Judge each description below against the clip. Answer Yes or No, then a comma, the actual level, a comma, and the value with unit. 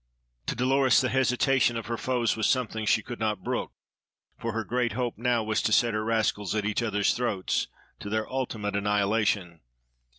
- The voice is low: Yes, low, 110 Hz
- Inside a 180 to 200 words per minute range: Yes, average, 185 wpm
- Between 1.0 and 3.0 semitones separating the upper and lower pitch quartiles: Yes, narrow, 2.6 semitones